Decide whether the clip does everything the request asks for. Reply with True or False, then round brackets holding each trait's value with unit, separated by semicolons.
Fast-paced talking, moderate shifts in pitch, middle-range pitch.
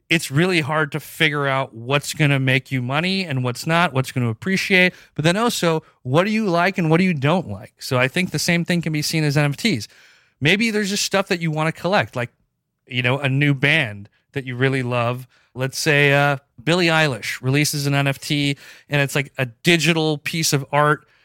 True (220 wpm; 4.1 semitones; 150 Hz)